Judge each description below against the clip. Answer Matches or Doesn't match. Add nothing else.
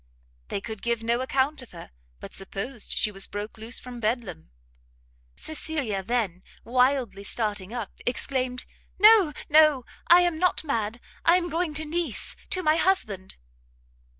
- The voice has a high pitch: Matches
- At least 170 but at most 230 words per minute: Doesn't match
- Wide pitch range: Matches